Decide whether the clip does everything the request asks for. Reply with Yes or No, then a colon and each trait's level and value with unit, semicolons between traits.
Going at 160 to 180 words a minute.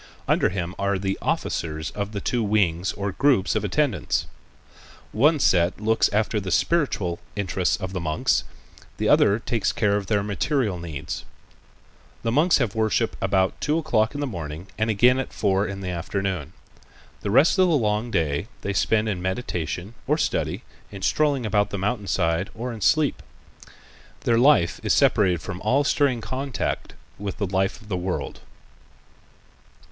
Yes: average, 170 wpm